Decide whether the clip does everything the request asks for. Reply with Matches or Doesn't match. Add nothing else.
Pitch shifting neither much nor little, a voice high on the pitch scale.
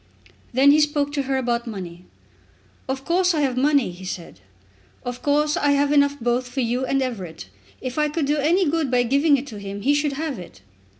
Matches